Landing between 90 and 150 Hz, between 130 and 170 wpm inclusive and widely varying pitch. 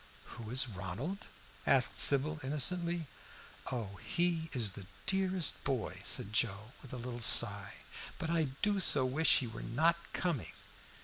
Yes: low, 135 Hz; average, 145 wpm; wide, 6.8 semitones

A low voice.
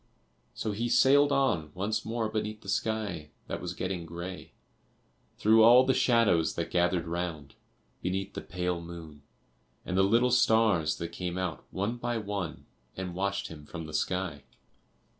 Yes: very low, 95 Hz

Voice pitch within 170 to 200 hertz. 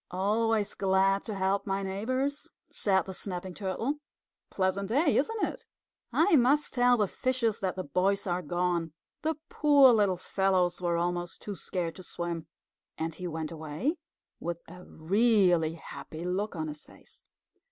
Yes: high, 190 Hz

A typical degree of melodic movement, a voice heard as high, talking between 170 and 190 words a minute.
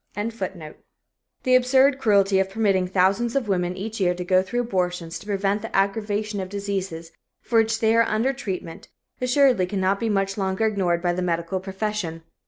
Yes: average, 3.3 semitones; high, 195 Hz; average, 180 wpm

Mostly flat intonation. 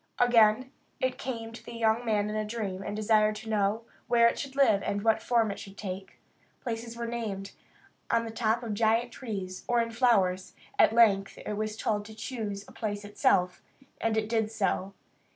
Yes: narrow, 2.2 semitones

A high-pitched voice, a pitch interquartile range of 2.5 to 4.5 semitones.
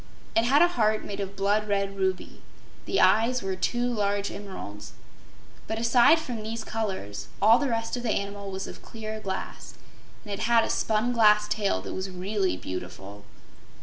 Yes: high, 210 Hz; average, 2.8 semitones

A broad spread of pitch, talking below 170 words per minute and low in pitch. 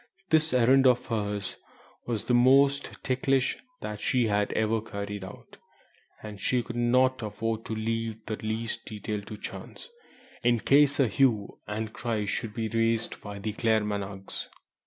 No: average, 2.9 semitones; average, 150 wpm; low, 115 Hz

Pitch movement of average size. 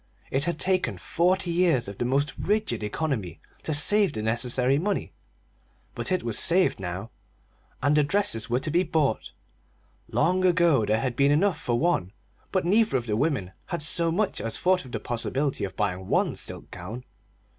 No: wide, 7.2 semitones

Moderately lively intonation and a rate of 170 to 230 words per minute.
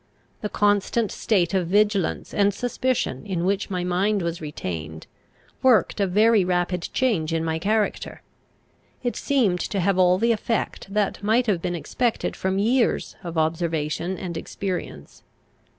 No: average, 3.7 semitones; average, 150 wpm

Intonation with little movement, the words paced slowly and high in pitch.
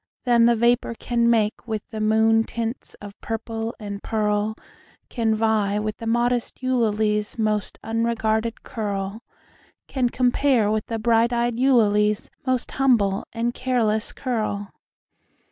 Yes: narrow, 1.9 semitones; slow, 130 wpm; high, 225 Hz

